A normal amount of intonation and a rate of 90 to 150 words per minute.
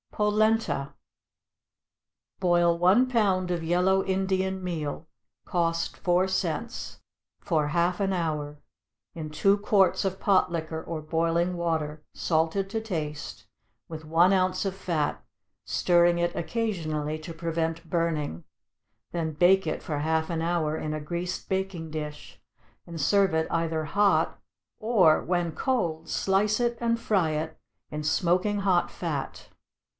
Yes: average, 3.1 semitones; slow, 135 wpm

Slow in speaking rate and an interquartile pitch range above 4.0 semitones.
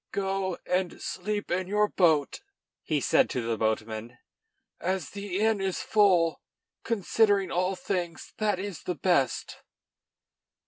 No: slow, 125 wpm; average, 3.4 semitones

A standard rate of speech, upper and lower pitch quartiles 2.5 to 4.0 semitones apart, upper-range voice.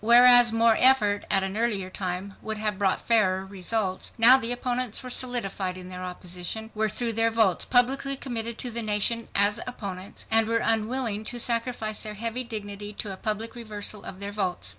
Yes: average, 185 wpm; average, 2.8 semitones; high, 220 Hz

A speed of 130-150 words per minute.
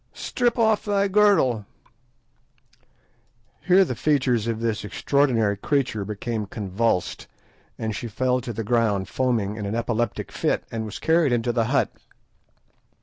Yes: average, 140 wpm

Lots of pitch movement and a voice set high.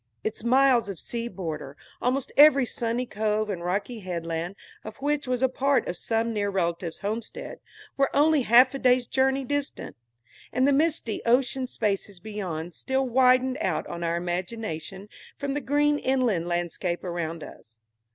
Yes: wide, 6.7 semitones; high, 230 Hz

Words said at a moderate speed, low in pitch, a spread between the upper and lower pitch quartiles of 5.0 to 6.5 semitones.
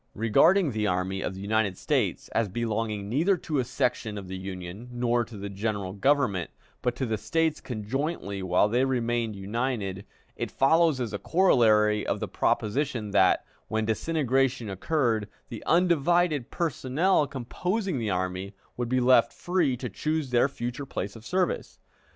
Yes: average, 160 wpm; low, 120 Hz; average, 5.3 semitones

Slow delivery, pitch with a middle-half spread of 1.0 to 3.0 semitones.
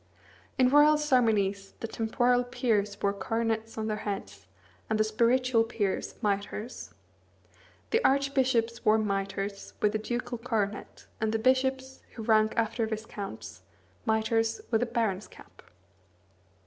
Yes: slow, 130 wpm; narrow, 2.6 semitones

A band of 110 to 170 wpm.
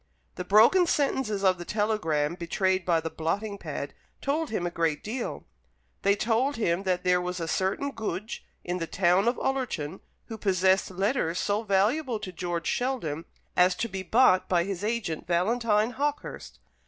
Yes: average, 165 wpm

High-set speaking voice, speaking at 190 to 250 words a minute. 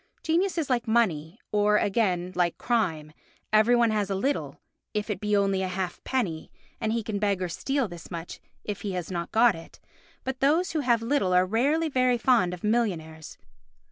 Yes: high, 210 Hz; average, 195 wpm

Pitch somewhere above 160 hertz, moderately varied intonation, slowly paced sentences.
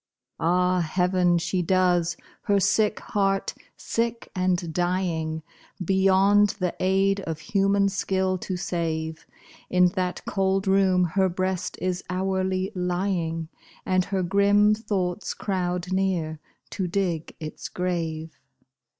No: medium, 185 Hz; narrow, 1.8 semitones; slow, 115 wpm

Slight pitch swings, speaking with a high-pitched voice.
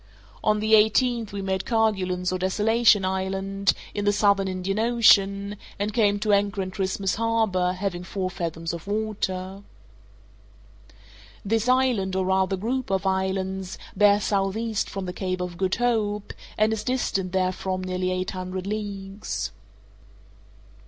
Yes: narrow, 2.2 semitones; high, 195 Hz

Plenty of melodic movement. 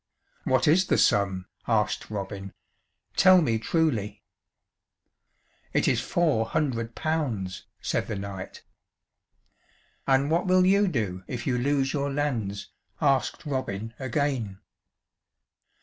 Yes: wide, 6.2 semitones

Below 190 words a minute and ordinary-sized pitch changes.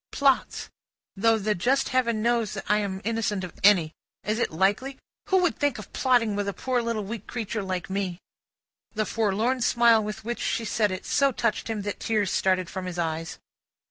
No: average, 195 wpm; average, 3.4 semitones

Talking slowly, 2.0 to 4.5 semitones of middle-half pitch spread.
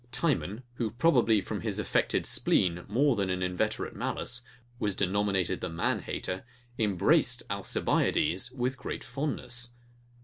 No: slow, 125 wpm; average, 5.0 semitones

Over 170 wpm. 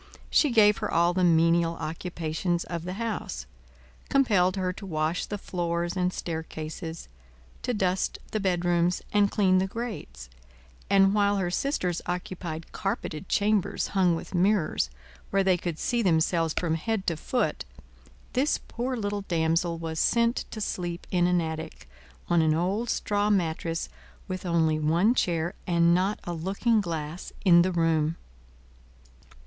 No: average, 150 wpm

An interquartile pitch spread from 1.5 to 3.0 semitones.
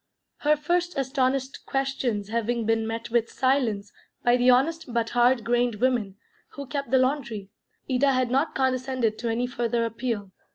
Yes: average, 2.7 semitones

